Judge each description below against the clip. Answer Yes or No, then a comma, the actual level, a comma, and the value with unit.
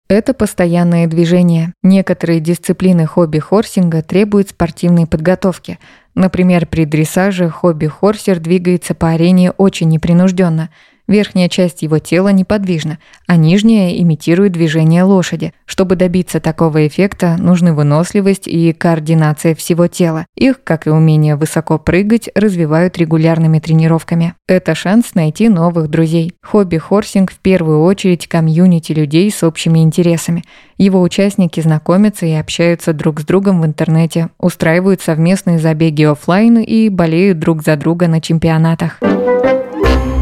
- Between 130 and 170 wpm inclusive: No, average, 120 wpm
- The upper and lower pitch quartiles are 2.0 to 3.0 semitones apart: Yes, narrow, 2.5 semitones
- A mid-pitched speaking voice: Yes, medium, 170 Hz